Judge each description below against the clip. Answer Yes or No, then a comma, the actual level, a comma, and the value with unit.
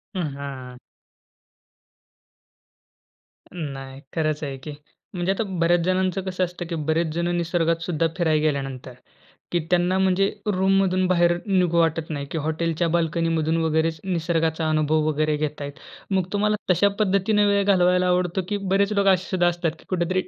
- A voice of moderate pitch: Yes, medium, 170 Hz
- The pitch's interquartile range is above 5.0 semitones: No, average, 2.9 semitones